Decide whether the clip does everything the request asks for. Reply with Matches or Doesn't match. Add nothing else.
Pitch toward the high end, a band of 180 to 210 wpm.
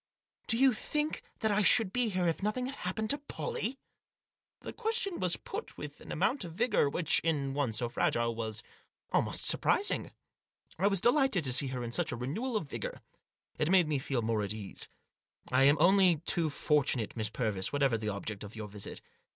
Doesn't match